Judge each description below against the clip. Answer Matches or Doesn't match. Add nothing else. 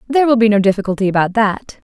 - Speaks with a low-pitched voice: Doesn't match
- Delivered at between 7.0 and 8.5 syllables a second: Matches